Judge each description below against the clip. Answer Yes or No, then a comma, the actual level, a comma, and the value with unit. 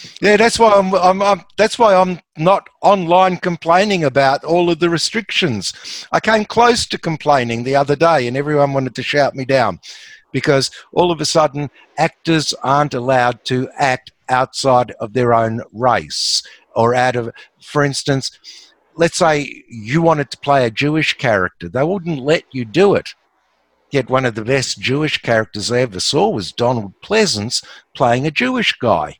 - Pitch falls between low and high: Yes, medium, 145 Hz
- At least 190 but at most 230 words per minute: No, average, 175 wpm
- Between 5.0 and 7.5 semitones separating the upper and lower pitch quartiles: Yes, wide, 5.4 semitones